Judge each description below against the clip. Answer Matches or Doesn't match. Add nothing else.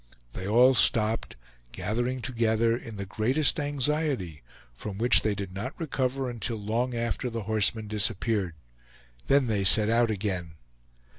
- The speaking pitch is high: Doesn't match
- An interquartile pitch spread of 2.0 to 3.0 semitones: Doesn't match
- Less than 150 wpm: Matches